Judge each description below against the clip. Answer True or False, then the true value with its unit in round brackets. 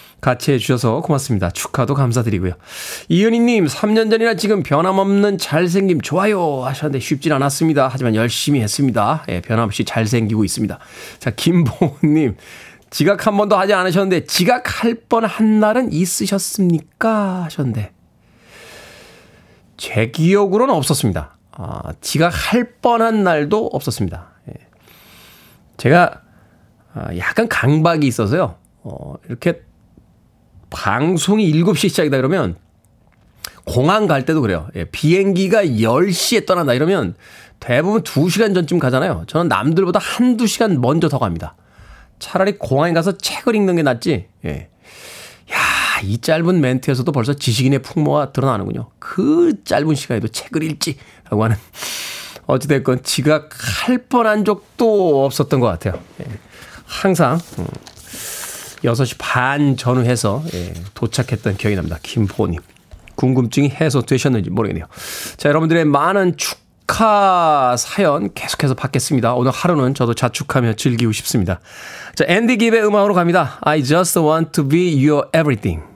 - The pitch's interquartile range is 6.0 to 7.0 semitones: False (7.7 semitones)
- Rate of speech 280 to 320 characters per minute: True (315 characters per minute)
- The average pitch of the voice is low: False (150 Hz)